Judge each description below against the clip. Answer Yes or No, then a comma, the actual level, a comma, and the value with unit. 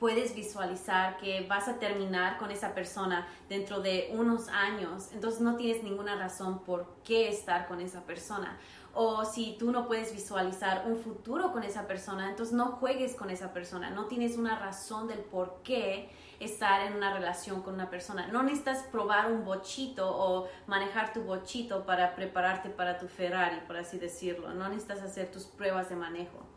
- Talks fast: No, average, 180 wpm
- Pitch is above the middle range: Yes, high, 195 Hz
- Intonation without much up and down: No, average, 3.1 semitones